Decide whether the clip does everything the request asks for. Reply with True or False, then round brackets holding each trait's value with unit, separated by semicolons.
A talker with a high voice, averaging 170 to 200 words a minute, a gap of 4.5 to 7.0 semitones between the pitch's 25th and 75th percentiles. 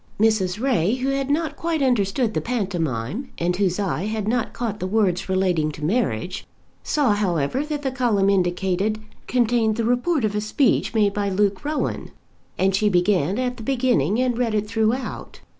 True (215 Hz; 180 wpm; 4.8 semitones)